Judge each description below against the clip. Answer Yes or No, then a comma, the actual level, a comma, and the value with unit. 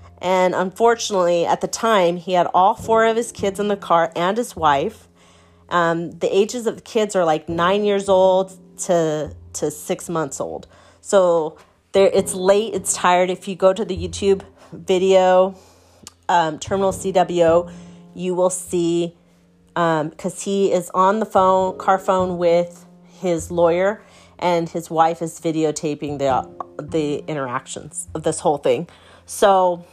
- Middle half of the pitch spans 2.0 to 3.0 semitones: Yes, narrow, 2.6 semitones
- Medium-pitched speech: Yes, medium, 180 Hz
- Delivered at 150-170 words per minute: Yes, average, 155 wpm